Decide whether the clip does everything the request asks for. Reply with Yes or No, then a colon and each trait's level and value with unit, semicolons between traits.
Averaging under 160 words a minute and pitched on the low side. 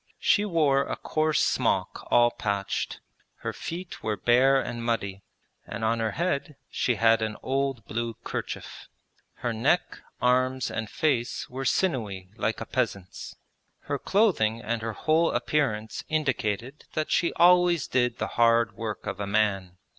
Yes: average, 150 wpm; low, 120 Hz